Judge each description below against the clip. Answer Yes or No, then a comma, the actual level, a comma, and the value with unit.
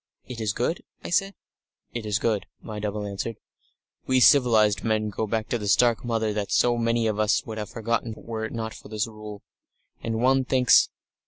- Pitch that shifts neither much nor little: No, narrow, 1.8 semitones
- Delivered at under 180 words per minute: No, average, 195 wpm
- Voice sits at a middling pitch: No, low, 110 Hz